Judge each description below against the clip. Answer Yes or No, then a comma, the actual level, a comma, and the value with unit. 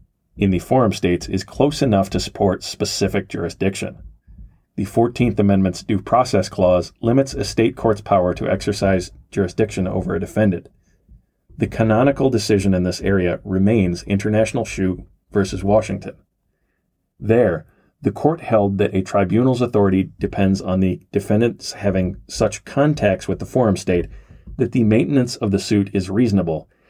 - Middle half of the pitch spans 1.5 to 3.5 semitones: Yes, average, 3.1 semitones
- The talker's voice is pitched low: Yes, low, 100 Hz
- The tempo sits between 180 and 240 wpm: No, average, 145 wpm